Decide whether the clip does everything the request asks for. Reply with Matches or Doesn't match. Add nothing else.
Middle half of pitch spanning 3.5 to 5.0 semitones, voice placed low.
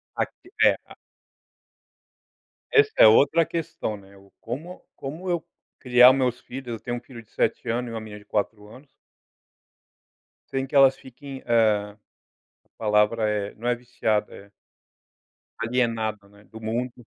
Matches